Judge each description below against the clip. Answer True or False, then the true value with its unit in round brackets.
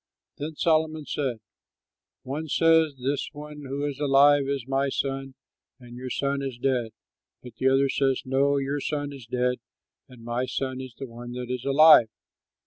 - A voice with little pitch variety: True (2.3 semitones)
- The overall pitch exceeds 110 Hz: True (135 Hz)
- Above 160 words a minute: True (170 wpm)